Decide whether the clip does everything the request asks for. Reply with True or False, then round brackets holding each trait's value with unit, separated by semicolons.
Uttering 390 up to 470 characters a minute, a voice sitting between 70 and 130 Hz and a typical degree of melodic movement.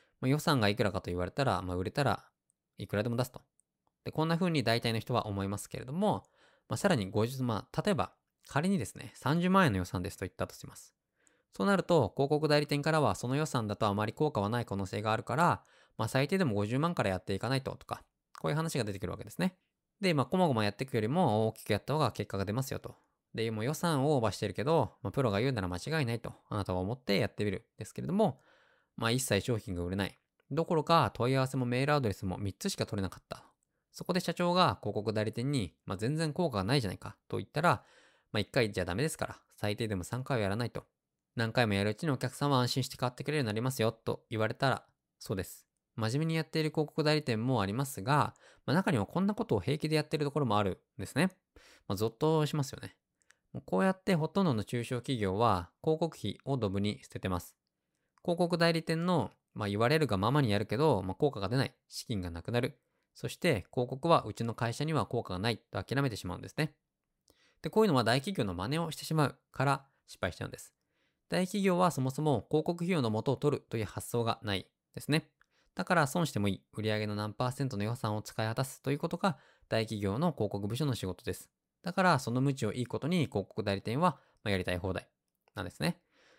False (445 characters per minute; 125 Hz; 6.6 semitones)